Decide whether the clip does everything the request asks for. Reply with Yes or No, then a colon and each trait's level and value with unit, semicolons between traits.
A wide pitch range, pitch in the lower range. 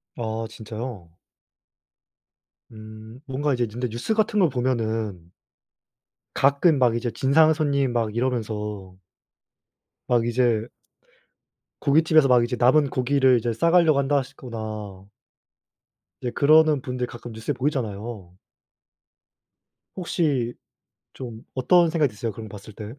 No: average, 4.1 semitones; low, 125 Hz